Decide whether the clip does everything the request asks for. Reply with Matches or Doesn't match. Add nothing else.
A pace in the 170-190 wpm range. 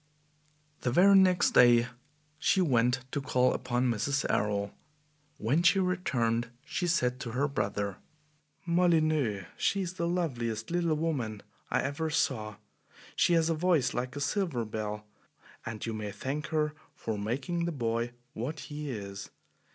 Doesn't match